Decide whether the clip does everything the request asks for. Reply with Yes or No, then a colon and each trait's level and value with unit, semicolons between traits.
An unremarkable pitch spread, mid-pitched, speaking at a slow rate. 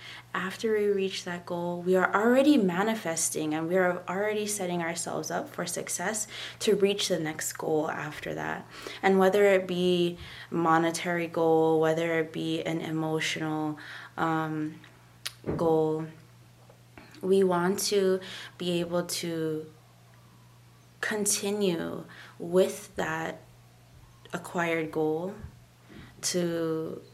Yes: average, 3.1 semitones; medium, 165 Hz; slow, 110 wpm